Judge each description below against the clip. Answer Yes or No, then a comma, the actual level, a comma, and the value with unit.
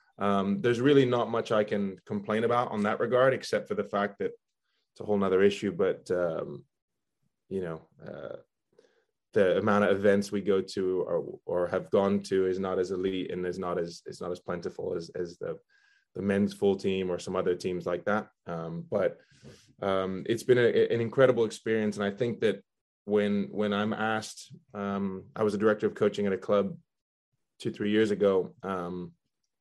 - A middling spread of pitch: No, wide, 6.4 semitones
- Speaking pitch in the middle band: No, low, 105 Hz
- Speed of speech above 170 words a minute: Yes, average, 195 wpm